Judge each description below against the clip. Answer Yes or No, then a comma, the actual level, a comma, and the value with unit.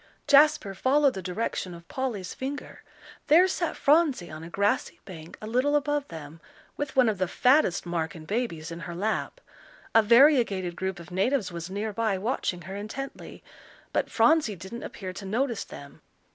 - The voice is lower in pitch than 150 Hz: No, high, 210 Hz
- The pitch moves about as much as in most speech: No, wide, 6.9 semitones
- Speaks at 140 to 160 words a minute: No, average, 170 wpm